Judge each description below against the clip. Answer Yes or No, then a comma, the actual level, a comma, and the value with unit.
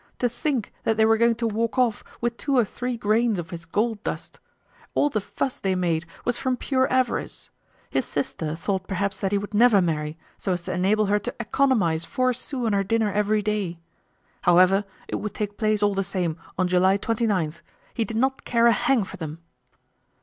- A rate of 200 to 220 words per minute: Yes, fast, 205 wpm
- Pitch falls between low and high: No, high, 210 Hz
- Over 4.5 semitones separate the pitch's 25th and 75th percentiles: No, average, 3.9 semitones